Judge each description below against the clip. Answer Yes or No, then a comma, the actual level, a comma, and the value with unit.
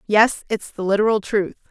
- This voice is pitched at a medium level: No, high, 205 Hz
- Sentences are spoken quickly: No, average, 175 wpm